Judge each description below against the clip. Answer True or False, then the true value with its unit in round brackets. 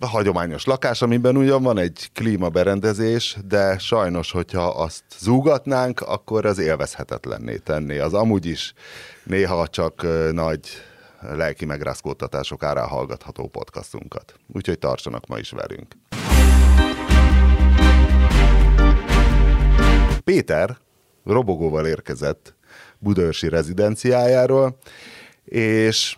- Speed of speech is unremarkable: False (90 wpm)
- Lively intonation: True (6.3 semitones)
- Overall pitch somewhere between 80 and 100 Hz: True (90 Hz)